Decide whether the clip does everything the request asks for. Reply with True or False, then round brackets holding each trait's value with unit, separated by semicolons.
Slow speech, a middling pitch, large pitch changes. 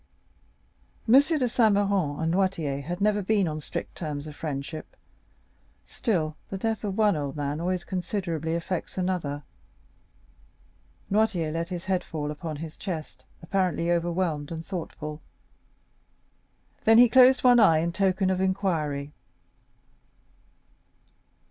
False (130 wpm; 175 Hz; 4.2 semitones)